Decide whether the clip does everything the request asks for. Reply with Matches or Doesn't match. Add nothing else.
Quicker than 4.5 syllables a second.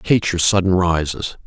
Matches